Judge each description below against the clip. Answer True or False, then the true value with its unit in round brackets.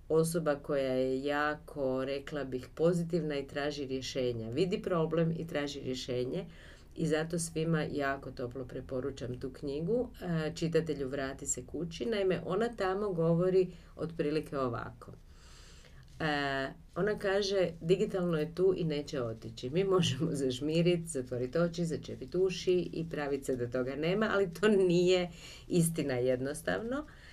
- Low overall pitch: False (150 Hz)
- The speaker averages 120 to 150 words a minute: True (135 wpm)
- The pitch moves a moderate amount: True (4.9 semitones)